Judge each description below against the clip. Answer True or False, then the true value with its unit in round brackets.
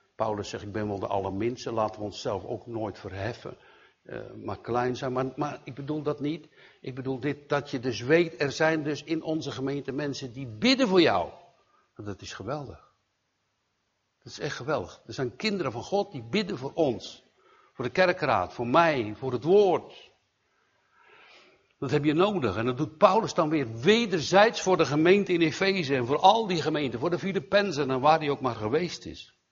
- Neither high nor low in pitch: True (145 Hz)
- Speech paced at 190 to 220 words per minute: True (195 wpm)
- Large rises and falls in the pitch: True (5.8 semitones)